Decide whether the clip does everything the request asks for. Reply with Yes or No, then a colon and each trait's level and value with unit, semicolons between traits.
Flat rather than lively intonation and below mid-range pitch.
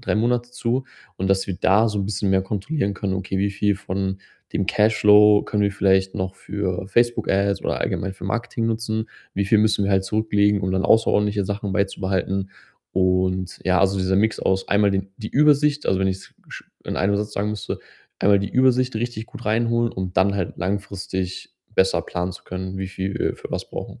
Yes: narrow, 2.2 semitones; low, 100 Hz